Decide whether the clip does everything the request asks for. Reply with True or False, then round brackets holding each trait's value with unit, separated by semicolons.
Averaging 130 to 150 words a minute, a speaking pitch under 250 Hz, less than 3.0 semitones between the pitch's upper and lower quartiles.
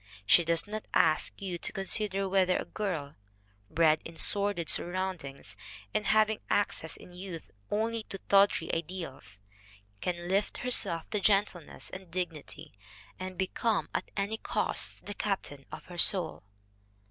False (140 wpm; 185 Hz; 3.4 semitones)